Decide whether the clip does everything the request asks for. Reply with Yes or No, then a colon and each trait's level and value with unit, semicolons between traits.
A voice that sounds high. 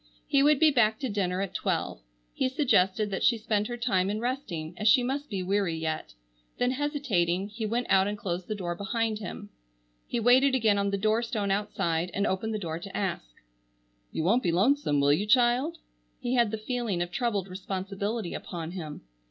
Yes: high, 205 Hz